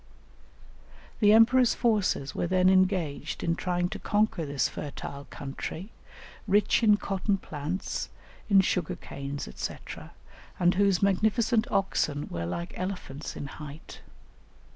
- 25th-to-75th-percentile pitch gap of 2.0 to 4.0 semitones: No, wide, 5.6 semitones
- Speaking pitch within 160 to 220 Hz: Yes, medium, 185 Hz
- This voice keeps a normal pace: No, slow, 120 wpm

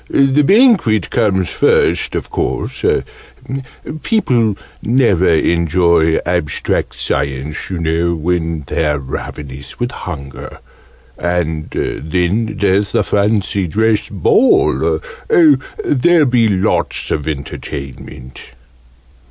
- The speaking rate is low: Yes, slow, 95 wpm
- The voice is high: No, very low, 90 Hz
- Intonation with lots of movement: Yes, wide, 6.0 semitones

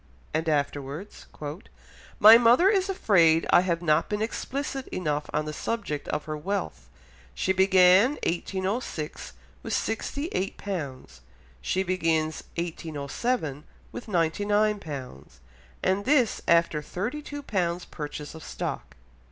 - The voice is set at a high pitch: No, medium, 180 Hz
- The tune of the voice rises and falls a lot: Yes, wide, 5.7 semitones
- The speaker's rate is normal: No, slow, 125 wpm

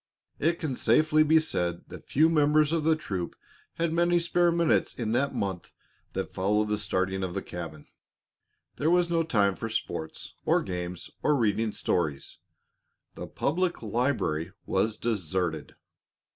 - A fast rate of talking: No, average, 150 wpm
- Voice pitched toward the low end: Yes, low, 115 Hz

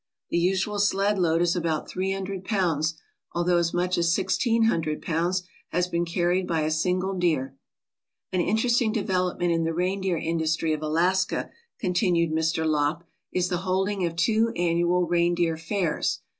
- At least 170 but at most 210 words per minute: No, average, 155 wpm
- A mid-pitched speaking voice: Yes, medium, 175 Hz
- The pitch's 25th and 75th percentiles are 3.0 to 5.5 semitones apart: No, narrow, 2.4 semitones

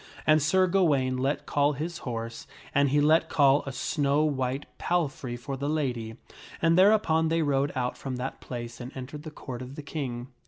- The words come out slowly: No, average, 190 wpm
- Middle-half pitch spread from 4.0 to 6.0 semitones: No, average, 3.4 semitones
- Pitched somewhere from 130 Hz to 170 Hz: Yes, medium, 140 Hz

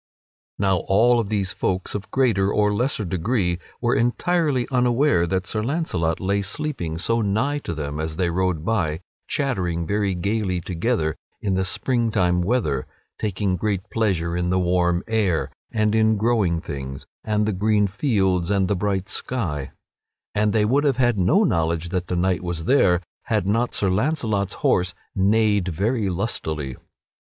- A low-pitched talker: Yes, low, 100 Hz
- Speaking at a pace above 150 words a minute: Yes, average, 160 wpm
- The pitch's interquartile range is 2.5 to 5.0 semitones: Yes, average, 4.2 semitones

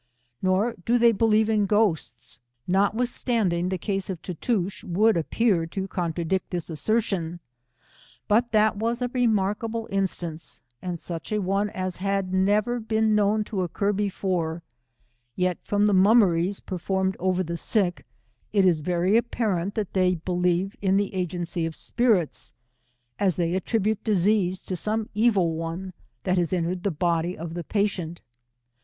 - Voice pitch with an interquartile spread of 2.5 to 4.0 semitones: Yes, average, 3.3 semitones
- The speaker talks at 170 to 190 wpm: No, average, 150 wpm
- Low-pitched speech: No, high, 190 Hz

